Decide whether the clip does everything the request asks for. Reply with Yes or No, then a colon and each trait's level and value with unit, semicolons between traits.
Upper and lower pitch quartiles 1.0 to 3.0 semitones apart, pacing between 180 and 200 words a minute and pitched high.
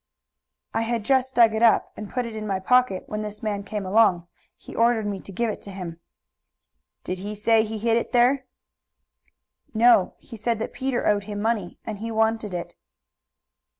Yes: narrow, 2.4 semitones; average, 190 wpm; high, 220 Hz